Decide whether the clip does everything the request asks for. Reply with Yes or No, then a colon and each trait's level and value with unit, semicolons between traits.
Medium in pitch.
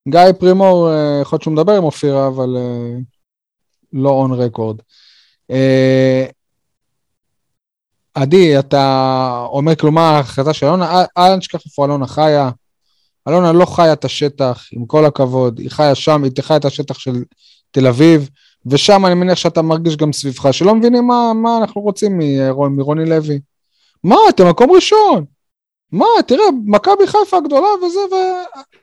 Yes: medium, 155 Hz